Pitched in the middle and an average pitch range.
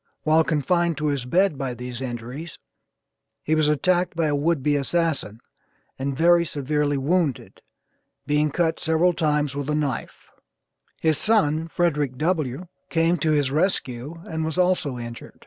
Yes: medium, 150 Hz; average, 3.2 semitones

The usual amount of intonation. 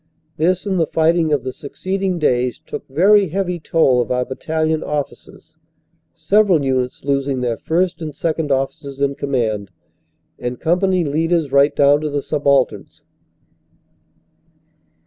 Yes: average, 3.9 semitones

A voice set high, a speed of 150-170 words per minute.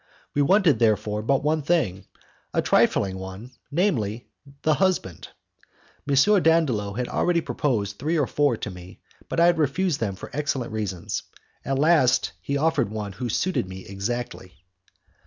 No: low, 125 Hz; average, 155 wpm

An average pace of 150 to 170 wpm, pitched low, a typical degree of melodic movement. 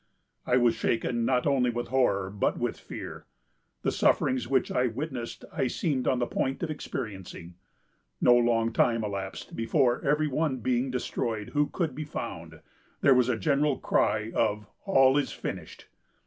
Yes: average, 160 wpm; low, 125 Hz; average, 3.1 semitones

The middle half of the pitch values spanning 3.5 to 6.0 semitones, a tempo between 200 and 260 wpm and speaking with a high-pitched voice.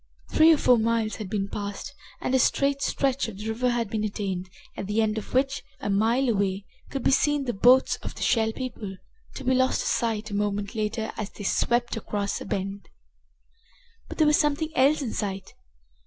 Yes: average, 4.2 semitones; fast, 205 wpm; high, 225 Hz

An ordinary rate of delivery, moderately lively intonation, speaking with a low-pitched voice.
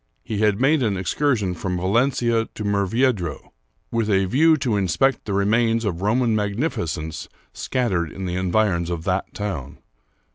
Yes: average, 155 wpm; average, 4.2 semitones; low, 105 Hz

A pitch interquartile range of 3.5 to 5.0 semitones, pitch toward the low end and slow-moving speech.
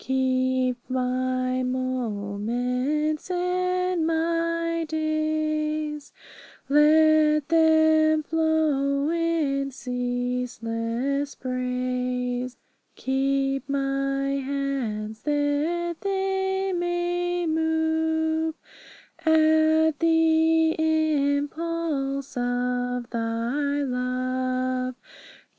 No: average, 3.9 semitones; very high, 285 Hz; slow, 60 wpm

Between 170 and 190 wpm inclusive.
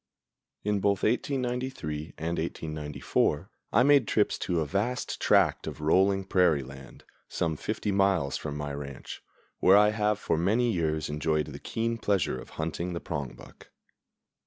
No: average, 150 wpm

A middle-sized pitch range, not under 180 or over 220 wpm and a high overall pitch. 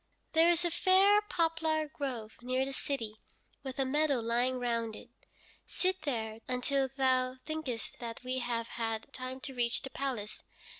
No: average, 4.6 semitones; average, 160 wpm; very high, 260 Hz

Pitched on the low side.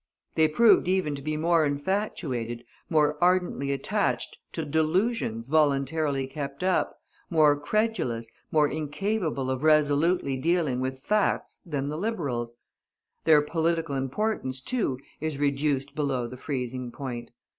No: medium, 150 Hz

